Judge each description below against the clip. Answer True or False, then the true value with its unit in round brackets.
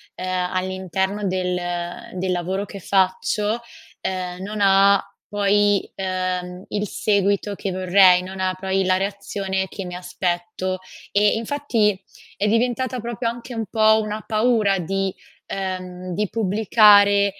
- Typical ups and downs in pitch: False (2.1 semitones)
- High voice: True (195 Hz)